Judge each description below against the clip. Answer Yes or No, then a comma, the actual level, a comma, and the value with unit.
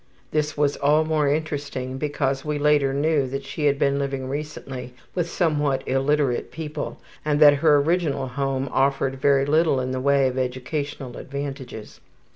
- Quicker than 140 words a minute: Yes, average, 170 wpm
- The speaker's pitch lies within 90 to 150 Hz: Yes, medium, 140 Hz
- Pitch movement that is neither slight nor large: No, narrow, 1.9 semitones